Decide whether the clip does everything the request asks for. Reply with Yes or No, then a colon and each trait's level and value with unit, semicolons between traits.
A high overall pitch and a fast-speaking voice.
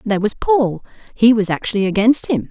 No: high, 220 Hz; average, 190 wpm